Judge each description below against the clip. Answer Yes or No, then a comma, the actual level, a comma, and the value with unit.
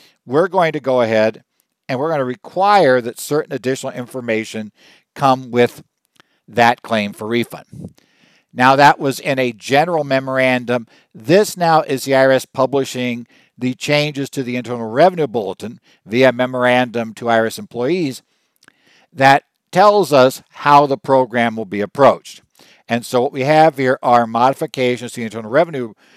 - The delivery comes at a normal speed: Yes, average, 150 wpm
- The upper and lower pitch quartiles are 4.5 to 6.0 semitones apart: No, average, 2.8 semitones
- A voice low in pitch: Yes, low, 130 Hz